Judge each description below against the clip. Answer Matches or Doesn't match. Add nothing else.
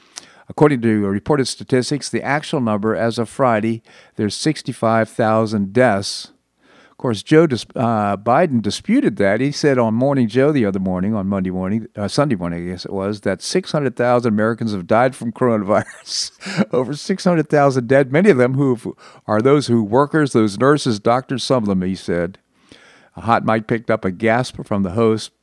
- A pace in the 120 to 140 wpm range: Doesn't match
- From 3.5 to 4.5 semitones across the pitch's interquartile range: Matches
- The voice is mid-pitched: Doesn't match